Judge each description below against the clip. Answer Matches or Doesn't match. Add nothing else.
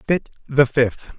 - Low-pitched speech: Matches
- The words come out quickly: Doesn't match